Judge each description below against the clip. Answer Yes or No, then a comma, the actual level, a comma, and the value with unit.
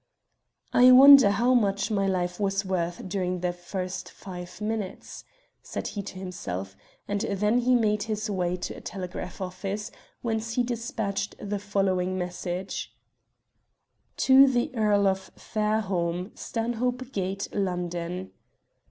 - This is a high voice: Yes, high, 200 Hz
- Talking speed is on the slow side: Yes, slow, 130 wpm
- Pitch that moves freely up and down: No, average, 3.3 semitones